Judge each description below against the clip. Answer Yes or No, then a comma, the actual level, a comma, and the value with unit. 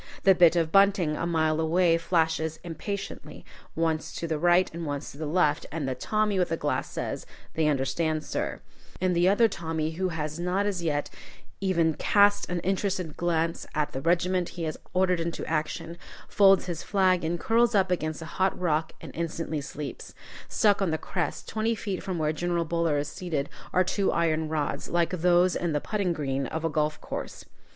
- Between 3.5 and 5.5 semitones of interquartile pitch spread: No, average, 2.7 semitones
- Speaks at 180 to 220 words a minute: Yes, average, 190 wpm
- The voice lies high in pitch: No, medium, 170 Hz